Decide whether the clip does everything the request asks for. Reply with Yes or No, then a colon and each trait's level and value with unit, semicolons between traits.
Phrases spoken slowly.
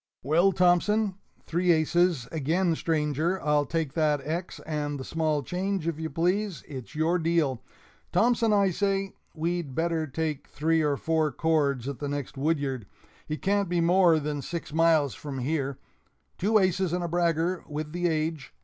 No: average, 165 wpm